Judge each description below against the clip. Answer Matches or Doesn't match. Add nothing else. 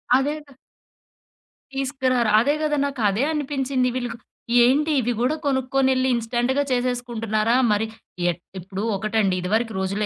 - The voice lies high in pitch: Matches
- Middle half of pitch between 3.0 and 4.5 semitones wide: Matches